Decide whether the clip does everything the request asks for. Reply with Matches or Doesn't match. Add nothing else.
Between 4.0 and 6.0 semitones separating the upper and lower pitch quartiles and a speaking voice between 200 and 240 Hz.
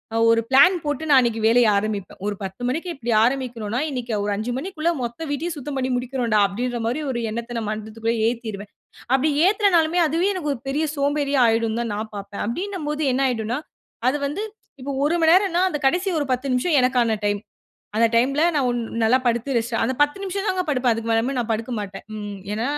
Doesn't match